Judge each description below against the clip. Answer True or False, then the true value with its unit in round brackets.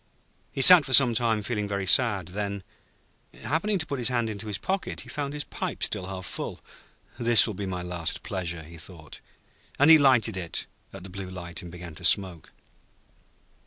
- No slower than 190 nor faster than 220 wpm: True (195 wpm)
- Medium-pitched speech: False (100 Hz)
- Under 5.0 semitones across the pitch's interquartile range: False (5.6 semitones)